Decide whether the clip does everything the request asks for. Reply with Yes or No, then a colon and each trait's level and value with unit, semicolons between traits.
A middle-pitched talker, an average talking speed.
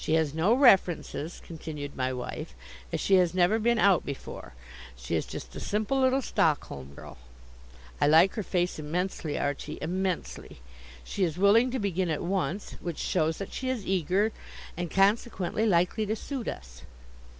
Yes: medium, 180 Hz; average, 165 wpm